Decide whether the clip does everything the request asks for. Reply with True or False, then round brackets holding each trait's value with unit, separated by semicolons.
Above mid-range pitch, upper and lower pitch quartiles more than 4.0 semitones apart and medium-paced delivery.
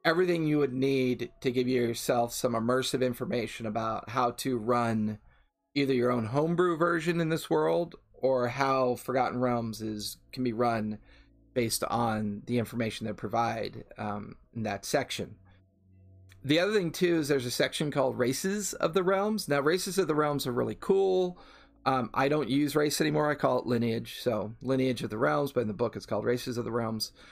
False (125 Hz; 4.4 semitones; 190 wpm)